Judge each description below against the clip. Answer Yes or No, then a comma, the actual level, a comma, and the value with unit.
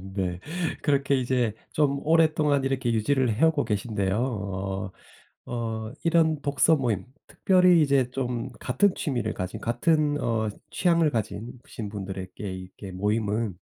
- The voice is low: Yes, low, 120 Hz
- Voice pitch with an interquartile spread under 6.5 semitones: Yes, wide, 5.6 semitones